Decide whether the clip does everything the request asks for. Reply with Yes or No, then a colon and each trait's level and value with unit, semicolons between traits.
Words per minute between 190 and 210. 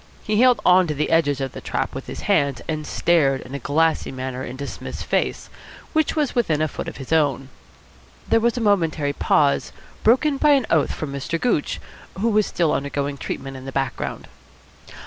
Yes: average, 195 wpm